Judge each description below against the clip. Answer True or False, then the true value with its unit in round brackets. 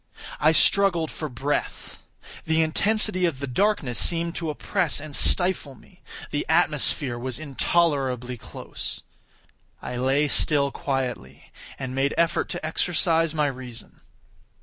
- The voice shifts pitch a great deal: False (4.2 semitones)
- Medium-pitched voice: True (150 Hz)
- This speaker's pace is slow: True (125 wpm)